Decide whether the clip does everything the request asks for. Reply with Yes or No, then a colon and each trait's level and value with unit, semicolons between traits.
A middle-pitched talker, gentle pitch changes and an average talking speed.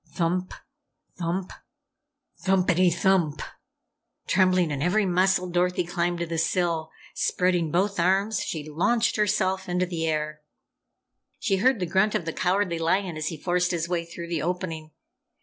Yes: medium, 180 Hz; narrow, 2.1 semitones; average, 150 wpm